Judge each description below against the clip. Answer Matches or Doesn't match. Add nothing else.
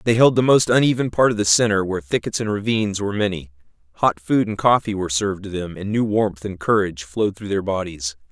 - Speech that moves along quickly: Matches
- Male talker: Matches